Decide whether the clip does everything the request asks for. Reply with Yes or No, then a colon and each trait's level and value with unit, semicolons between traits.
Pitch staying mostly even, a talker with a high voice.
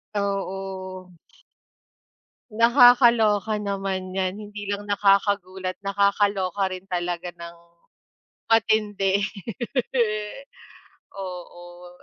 Yes: narrow, 1.8 semitones; high, 195 Hz